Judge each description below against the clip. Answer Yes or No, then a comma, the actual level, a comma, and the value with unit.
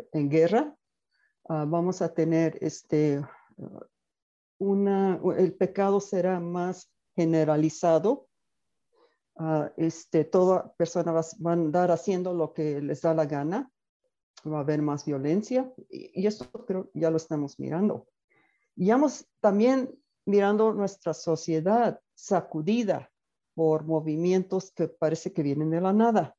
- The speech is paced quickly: No, average, 130 wpm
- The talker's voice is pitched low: No, medium, 175 Hz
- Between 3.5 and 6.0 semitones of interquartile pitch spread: Yes, average, 4.1 semitones